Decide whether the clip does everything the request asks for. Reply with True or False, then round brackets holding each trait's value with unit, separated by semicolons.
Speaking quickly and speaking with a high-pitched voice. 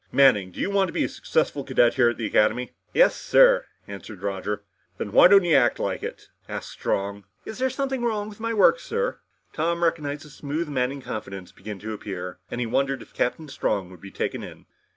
False (215 wpm; 135 Hz)